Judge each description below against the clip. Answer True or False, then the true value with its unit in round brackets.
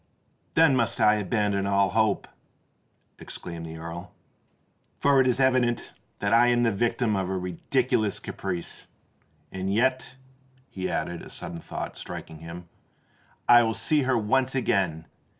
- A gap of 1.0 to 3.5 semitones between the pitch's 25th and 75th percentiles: False (5.2 semitones)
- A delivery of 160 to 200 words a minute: False (145 wpm)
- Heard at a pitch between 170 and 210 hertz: False (105 Hz)